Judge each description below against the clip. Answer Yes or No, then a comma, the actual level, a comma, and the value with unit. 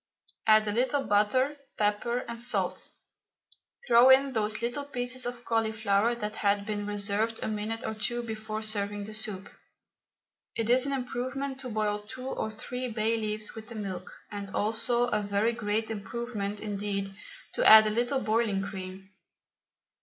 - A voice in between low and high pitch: No, high, 220 Hz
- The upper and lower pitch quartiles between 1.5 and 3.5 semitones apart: Yes, narrow, 2.6 semitones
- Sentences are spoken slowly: No, average, 160 wpm